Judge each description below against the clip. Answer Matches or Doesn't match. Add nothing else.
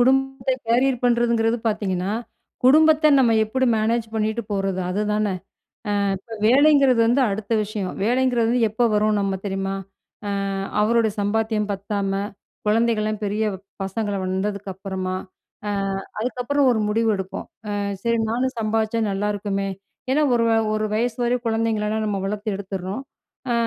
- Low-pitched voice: Doesn't match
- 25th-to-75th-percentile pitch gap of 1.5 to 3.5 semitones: Matches